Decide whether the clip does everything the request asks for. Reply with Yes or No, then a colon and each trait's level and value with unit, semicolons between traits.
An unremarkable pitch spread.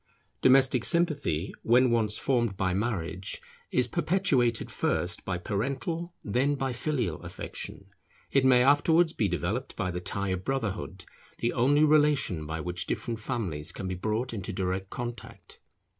No: wide, 6.2 semitones